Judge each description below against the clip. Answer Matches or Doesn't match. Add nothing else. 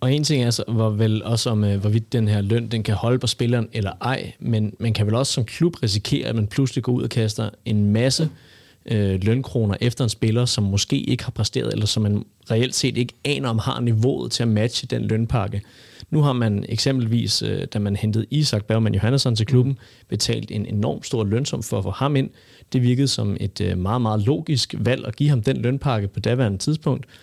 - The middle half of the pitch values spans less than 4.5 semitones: Matches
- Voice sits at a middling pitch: Doesn't match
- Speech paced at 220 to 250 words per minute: Matches